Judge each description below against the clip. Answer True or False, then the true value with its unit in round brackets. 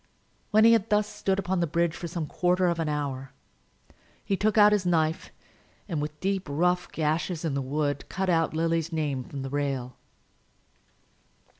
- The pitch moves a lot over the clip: False (3.8 semitones)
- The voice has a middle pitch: True (165 Hz)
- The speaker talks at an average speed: True (175 wpm)